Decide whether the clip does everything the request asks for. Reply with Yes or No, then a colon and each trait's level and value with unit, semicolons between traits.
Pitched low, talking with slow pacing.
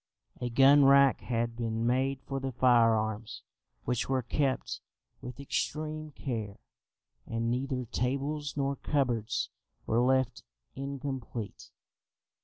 Yes: low, 130 Hz; slow, 110 wpm